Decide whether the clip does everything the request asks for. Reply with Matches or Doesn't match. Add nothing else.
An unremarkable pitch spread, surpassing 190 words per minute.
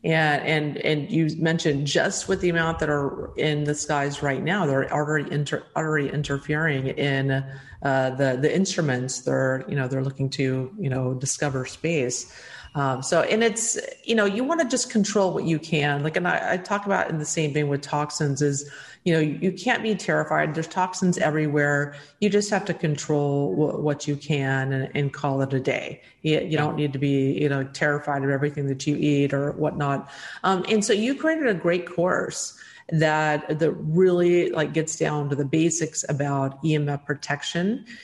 Matches